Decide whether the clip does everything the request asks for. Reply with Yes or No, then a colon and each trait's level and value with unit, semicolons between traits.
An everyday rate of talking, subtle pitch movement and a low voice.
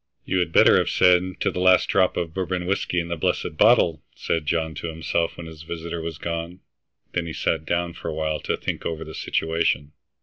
No: fast, 215 wpm; narrow, 1.7 semitones; very low, 85 Hz